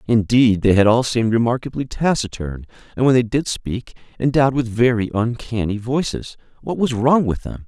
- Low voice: Yes, low, 120 Hz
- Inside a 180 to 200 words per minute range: No, average, 170 wpm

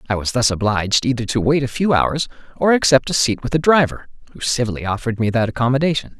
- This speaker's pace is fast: Yes, fast, 225 wpm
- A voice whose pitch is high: No, low, 125 Hz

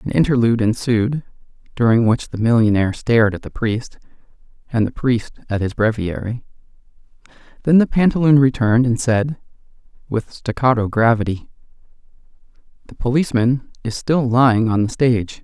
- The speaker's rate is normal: No, slow, 130 wpm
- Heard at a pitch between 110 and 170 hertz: Yes, low, 120 Hz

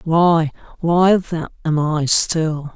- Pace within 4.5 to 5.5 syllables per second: No, 2.8 syllables/s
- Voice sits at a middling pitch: Yes, medium, 160 Hz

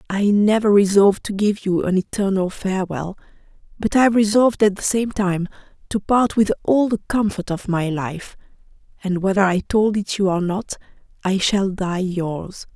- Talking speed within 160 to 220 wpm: Yes, average, 175 wpm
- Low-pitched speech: No, high, 195 Hz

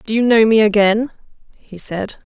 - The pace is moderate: Yes, average, 180 wpm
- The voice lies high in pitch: Yes, high, 215 Hz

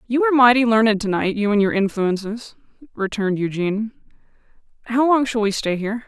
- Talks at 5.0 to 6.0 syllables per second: No, 6.2 syllables/s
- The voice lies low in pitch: No, high, 220 Hz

